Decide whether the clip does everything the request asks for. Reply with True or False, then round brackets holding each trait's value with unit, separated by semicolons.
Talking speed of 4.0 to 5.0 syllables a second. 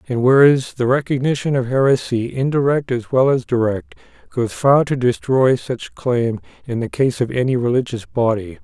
True (4.8 syllables/s)